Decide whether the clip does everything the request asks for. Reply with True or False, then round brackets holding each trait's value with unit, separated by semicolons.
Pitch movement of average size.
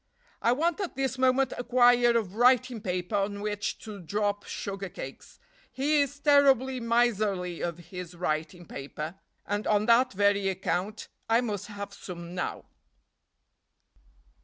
True (5.0 semitones)